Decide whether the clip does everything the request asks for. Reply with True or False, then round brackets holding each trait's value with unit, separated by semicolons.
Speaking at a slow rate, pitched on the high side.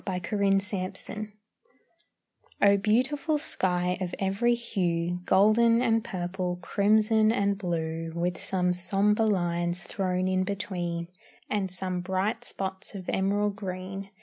True (120 wpm; 195 Hz)